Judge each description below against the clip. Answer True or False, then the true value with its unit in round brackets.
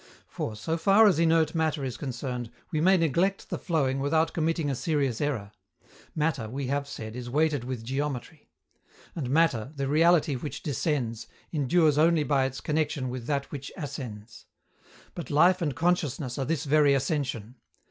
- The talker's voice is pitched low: False (145 Hz)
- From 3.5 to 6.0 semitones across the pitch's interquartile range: True (3.8 semitones)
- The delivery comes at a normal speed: True (165 wpm)